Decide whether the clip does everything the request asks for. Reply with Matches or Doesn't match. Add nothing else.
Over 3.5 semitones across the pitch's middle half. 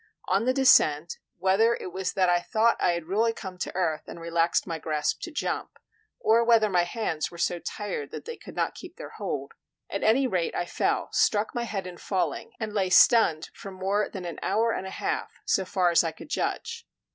Matches